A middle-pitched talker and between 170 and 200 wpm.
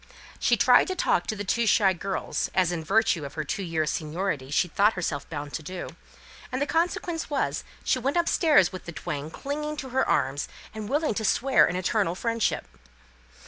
No: high, 200 Hz; average, 195 wpm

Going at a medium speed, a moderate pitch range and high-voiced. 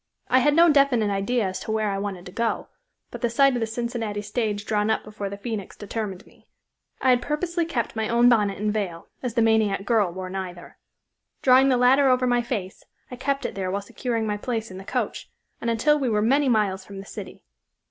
No: fast, 225 wpm; average, 3.7 semitones; high, 220 Hz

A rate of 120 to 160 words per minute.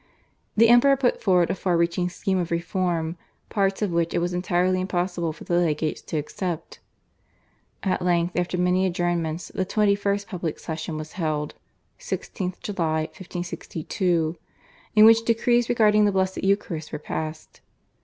Yes: average, 150 wpm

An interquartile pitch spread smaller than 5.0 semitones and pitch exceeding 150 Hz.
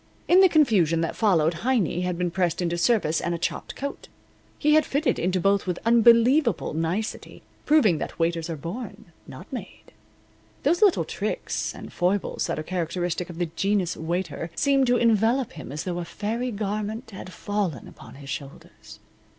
No: wide, 5.6 semitones; medium, 185 Hz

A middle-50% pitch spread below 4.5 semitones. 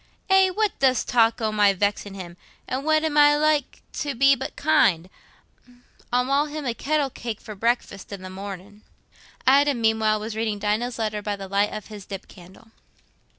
No: average, 5.3 semitones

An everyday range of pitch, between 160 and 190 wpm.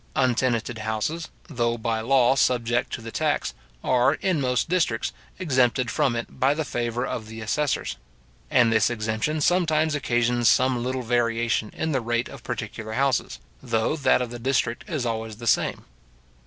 Yes: average, 3.0 semitones; average, 165 wpm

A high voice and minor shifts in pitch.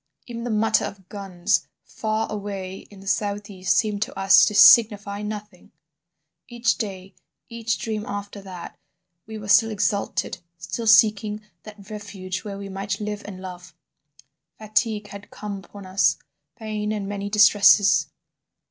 Yes: high, 205 Hz; narrow, 1.5 semitones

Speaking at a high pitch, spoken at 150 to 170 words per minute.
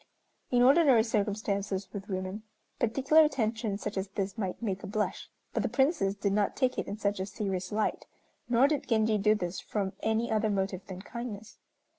No: high, 210 Hz; average, 185 wpm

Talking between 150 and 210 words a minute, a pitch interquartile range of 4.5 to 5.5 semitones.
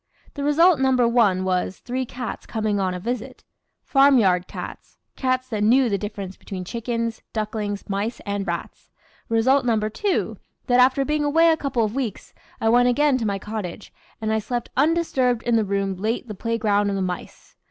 No: average, 185 wpm; average, 4.1 semitones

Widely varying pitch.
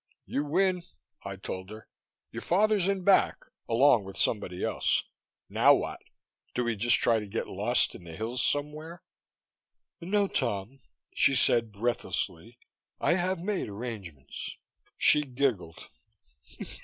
Yes: wide, 8.4 semitones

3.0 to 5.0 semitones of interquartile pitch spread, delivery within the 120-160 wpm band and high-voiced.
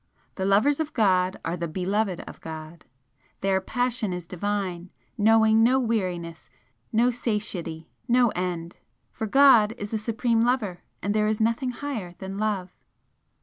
Yes: average, 4.2 semitones; average, 150 wpm; high, 205 Hz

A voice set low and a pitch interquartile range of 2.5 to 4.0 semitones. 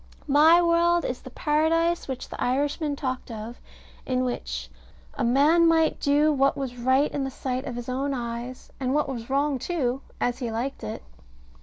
No: very high, 270 Hz; average, 3.4 semitones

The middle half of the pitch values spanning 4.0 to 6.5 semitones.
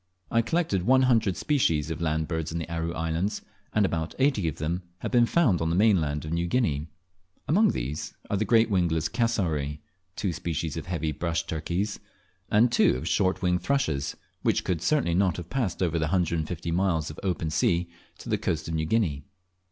Yes: average, 4.7 semitones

